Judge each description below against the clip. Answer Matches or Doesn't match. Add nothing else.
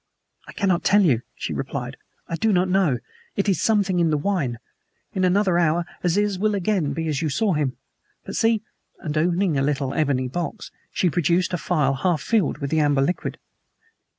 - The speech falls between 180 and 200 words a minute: Matches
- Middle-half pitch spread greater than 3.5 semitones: Matches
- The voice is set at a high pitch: Doesn't match